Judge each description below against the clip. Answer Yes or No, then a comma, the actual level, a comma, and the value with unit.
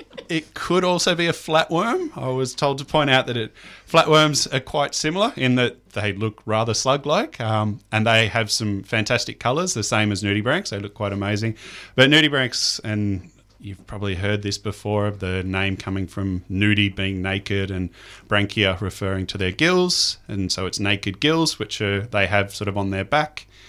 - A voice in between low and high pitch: No, low, 105 Hz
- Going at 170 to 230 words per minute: Yes, average, 190 wpm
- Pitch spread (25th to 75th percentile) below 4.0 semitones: No, average, 5.0 semitones